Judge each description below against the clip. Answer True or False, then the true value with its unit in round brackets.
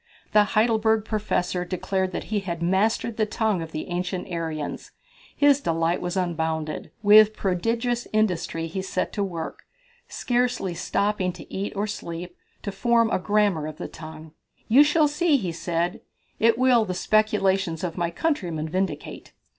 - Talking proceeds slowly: False (155 wpm)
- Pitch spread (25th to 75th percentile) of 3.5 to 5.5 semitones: True (4.2 semitones)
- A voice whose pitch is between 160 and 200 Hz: True (190 Hz)